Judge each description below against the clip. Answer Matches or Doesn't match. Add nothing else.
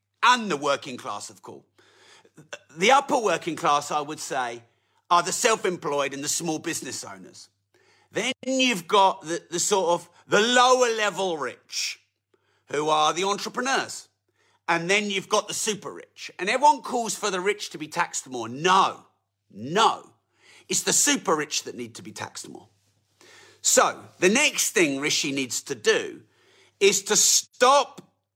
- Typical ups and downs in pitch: Doesn't match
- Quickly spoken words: Doesn't match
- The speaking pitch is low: Doesn't match